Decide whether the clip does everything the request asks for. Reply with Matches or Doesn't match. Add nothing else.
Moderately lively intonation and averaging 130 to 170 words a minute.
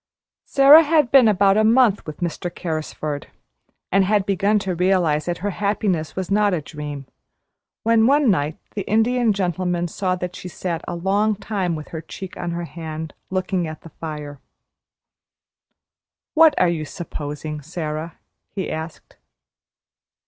Matches